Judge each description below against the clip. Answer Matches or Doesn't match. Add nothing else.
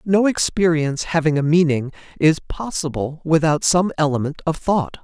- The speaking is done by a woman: Doesn't match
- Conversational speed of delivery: Matches